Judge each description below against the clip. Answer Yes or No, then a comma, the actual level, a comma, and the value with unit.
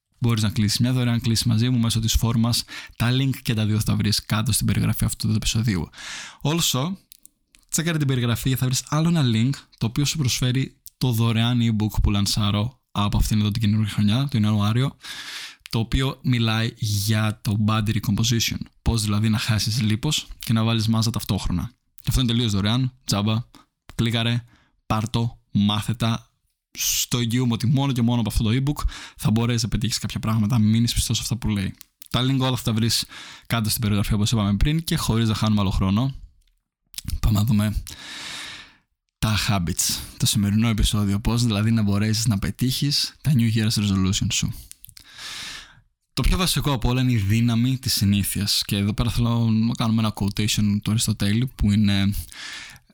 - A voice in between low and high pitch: No, low, 115 Hz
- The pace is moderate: No, fast, 180 wpm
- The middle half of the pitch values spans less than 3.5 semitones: Yes, narrow, 2.5 semitones